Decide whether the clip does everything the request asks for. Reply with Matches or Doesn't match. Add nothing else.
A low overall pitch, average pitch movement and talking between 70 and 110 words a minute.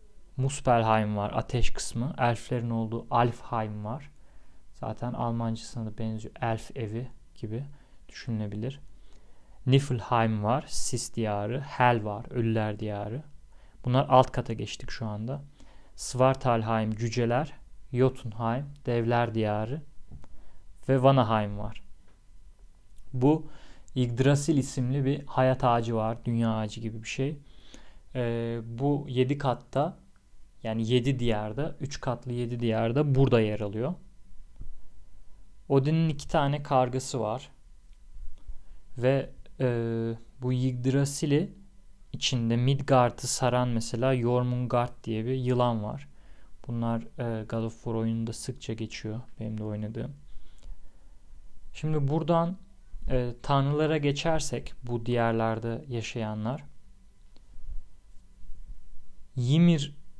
Matches